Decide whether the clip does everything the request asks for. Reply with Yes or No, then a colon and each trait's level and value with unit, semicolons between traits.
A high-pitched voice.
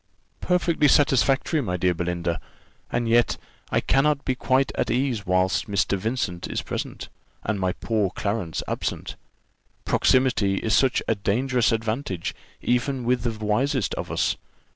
No: low, 115 Hz